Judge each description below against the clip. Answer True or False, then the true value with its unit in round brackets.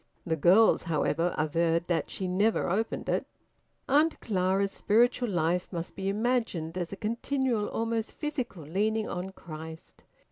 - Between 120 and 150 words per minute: True (140 wpm)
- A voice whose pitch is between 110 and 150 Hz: False (195 Hz)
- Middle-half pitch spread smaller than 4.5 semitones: False (5.0 semitones)